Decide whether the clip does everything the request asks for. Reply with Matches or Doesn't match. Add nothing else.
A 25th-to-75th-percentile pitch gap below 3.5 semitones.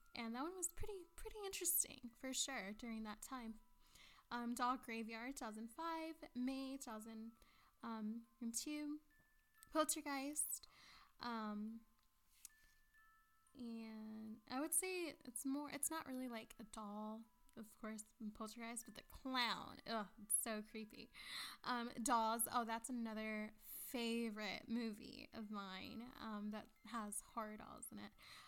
Doesn't match